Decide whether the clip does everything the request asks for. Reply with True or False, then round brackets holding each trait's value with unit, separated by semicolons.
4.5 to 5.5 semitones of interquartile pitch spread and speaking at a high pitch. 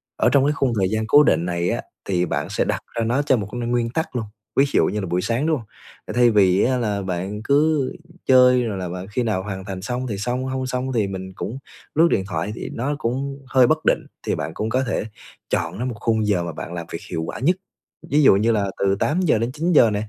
False (5.1 semitones; 115 Hz)